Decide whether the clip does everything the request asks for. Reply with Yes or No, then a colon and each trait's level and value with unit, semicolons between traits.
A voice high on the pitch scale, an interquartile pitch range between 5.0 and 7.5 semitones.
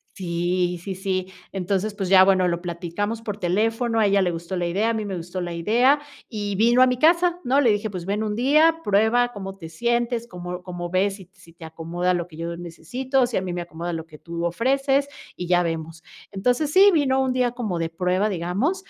Yes: high, 195 Hz; wide, 5.4 semitones